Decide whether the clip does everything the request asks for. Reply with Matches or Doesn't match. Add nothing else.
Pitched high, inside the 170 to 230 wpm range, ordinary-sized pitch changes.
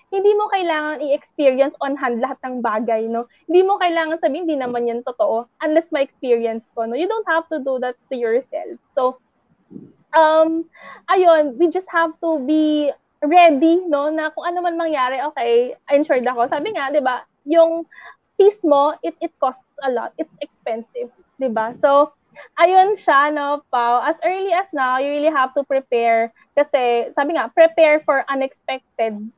Matches